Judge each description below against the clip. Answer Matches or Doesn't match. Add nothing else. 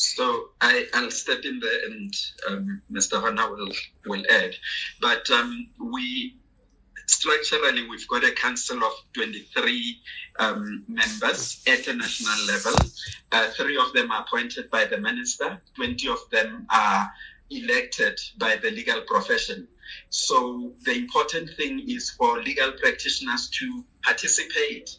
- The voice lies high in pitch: Matches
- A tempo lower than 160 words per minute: Matches